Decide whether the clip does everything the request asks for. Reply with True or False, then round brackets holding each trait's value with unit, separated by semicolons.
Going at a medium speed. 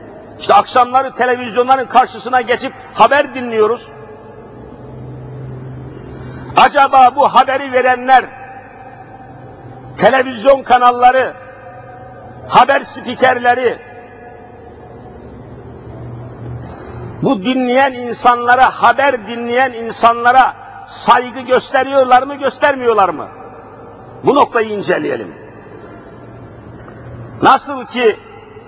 False (65 wpm)